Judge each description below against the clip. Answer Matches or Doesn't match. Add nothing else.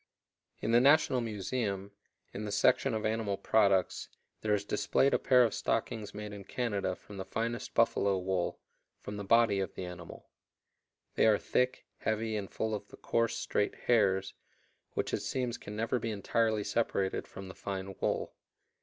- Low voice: Matches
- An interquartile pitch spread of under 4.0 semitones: Matches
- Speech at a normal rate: Matches